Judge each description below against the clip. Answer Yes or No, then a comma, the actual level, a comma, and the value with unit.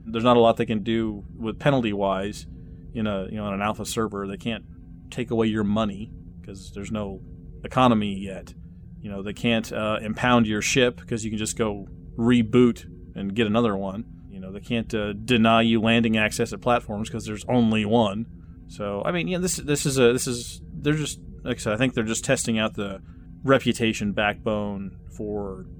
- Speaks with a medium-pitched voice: No, low, 110 Hz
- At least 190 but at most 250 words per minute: Yes, average, 200 wpm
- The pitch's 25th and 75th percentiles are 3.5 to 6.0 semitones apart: No, average, 3.1 semitones